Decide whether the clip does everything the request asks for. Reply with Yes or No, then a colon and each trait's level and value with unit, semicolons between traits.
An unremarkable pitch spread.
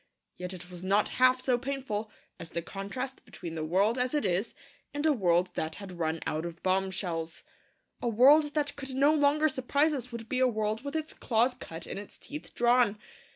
No: wide, 6.6 semitones